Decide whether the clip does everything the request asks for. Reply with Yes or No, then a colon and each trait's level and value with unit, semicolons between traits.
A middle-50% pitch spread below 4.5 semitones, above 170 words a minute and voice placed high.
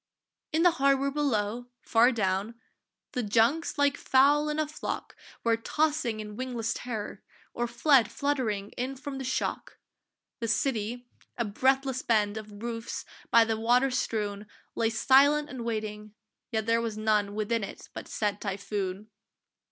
No: average, 4.0 semitones; average, 150 wpm; high, 230 Hz